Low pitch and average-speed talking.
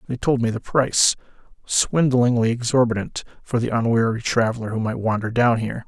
Yes: low, 120 Hz; average, 155 wpm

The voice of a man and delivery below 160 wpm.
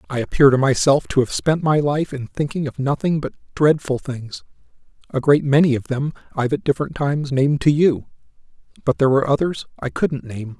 No: male; average, 200 wpm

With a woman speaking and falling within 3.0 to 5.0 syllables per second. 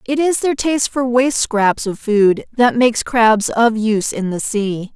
Yes: female; 4.5 syllables/s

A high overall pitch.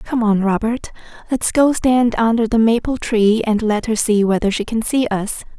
Yes: high, 225 Hz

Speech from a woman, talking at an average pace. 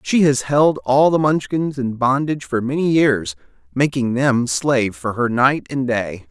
No: male; average, 180 wpm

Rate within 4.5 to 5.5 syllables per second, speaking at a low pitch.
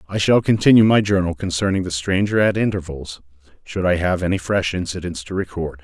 No: 5.7 syllables/s; very low, 90 Hz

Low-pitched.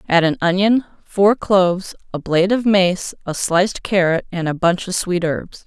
No: medium, 185 Hz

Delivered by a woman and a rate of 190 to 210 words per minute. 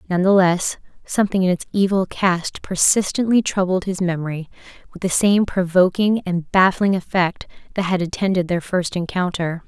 No: female; average, 155 wpm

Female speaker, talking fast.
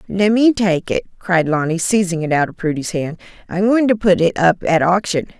Yes: female; fast, 225 wpm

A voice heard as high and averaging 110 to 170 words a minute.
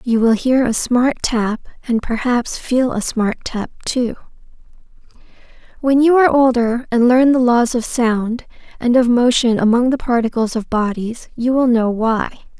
Yes: high, 240 Hz; average, 165 wpm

